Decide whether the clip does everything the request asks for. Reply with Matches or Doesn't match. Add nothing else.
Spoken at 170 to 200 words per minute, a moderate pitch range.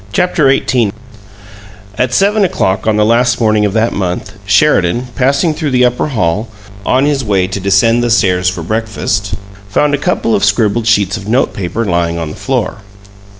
Matches